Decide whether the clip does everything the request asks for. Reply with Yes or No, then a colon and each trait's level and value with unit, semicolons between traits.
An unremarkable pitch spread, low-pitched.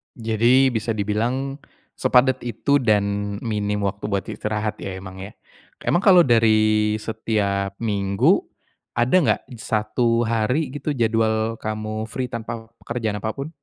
No: narrow, 2.3 semitones; low, 110 Hz